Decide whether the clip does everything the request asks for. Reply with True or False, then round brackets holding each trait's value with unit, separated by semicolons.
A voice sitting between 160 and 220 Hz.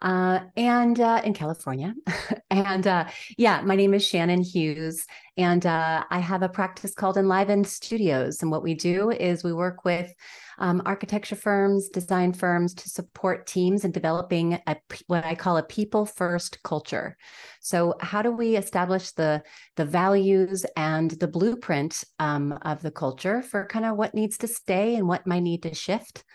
True (185 Hz)